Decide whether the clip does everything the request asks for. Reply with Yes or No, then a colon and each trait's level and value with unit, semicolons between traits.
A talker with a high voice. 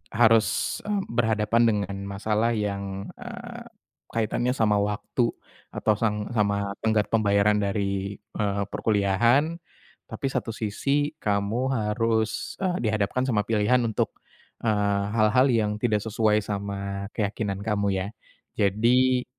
No: low, 105 Hz